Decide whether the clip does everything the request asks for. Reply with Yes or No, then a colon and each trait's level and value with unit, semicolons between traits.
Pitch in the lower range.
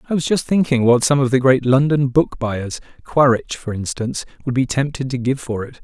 Yes: low, 130 Hz